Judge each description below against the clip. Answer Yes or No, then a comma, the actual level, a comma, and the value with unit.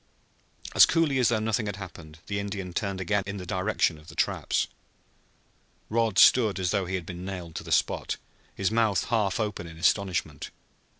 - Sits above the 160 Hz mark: No, low, 100 Hz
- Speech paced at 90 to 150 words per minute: No, average, 185 wpm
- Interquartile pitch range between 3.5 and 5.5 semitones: No, average, 3.1 semitones